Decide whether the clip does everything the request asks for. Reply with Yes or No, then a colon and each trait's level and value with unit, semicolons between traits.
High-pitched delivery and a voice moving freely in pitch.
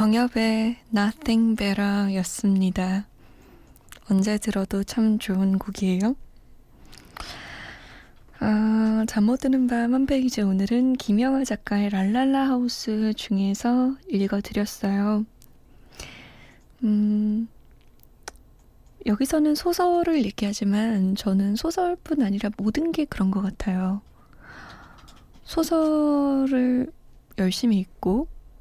No: high, 220 Hz; average, 4.2 semitones